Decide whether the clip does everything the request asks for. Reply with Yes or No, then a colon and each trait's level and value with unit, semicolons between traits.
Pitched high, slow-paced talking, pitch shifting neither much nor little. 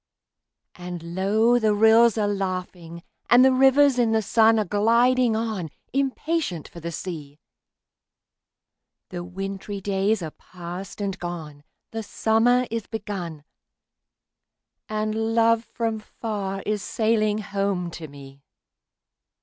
Yes: high, 205 Hz; slow, 120 wpm; average, 4.0 semitones